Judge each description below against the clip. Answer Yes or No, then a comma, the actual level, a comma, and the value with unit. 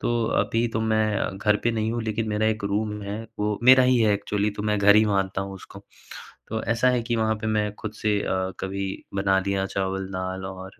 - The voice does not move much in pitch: Yes, narrow, 2.1 semitones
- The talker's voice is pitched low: Yes, low, 105 Hz